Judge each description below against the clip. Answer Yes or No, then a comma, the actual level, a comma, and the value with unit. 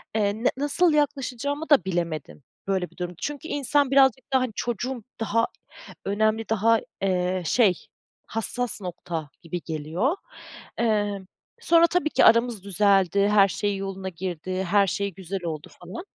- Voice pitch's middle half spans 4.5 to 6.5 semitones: Yes, average, 5.2 semitones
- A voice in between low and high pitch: No, high, 205 Hz